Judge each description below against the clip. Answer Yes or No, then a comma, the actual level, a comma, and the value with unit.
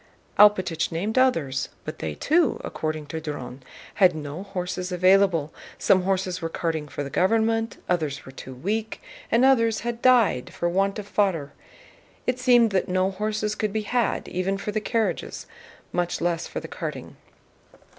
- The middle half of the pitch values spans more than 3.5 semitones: Yes, average, 4.9 semitones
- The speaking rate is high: No, average, 165 wpm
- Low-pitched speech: No, high, 190 Hz